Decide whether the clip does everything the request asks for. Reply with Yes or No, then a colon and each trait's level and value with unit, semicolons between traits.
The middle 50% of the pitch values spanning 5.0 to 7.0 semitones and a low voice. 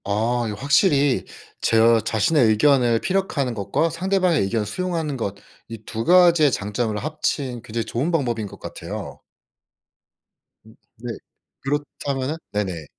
Yes: wide, 5.6 semitones; low, 125 Hz